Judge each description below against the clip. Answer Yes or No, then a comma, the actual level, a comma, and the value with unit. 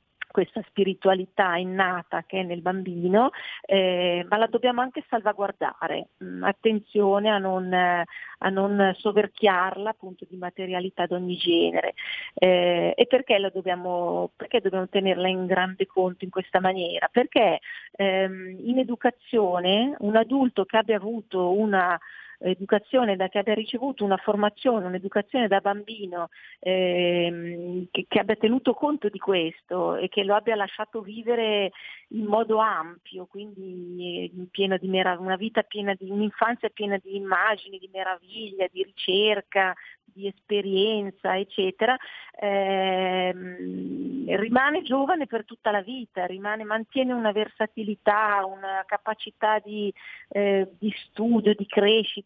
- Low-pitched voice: No, high, 200 Hz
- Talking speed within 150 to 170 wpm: No, average, 130 wpm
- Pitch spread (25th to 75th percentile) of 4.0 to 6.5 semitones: No, average, 2.8 semitones